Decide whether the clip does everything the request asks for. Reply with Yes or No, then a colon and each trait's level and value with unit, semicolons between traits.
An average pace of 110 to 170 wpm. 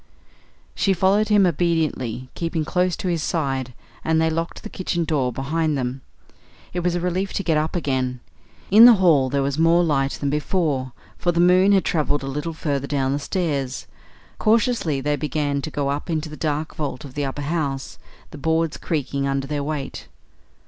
No: average, 190 wpm